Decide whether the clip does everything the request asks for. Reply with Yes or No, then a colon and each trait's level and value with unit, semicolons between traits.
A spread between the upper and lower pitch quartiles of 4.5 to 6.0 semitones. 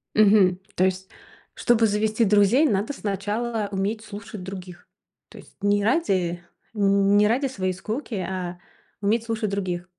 No: narrow, 2.6 semitones